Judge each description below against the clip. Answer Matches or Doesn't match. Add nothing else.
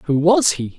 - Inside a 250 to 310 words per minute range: Doesn't match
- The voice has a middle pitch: Matches